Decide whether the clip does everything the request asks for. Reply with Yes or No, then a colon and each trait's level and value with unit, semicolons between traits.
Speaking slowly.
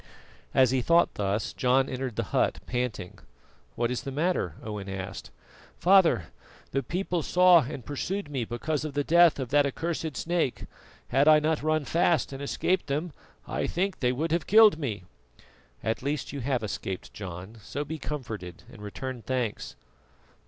No: average, 165 wpm